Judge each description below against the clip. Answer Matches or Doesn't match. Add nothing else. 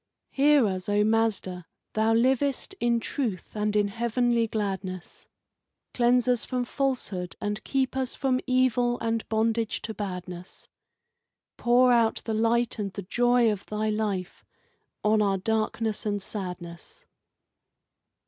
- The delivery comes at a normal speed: Doesn't match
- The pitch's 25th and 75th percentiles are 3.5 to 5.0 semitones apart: Doesn't match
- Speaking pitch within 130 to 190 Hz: Doesn't match